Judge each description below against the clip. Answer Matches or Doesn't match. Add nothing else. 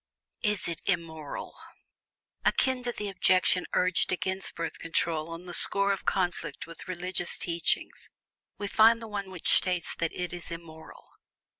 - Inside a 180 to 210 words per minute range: Doesn't match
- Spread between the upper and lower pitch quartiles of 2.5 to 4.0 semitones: Matches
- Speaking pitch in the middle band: Matches